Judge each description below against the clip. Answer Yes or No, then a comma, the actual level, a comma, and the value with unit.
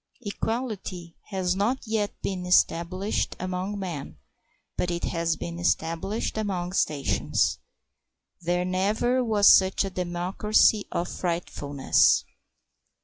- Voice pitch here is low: No, medium, 185 Hz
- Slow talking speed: Yes, slow, 105 wpm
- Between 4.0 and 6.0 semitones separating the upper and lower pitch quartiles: No, average, 3.0 semitones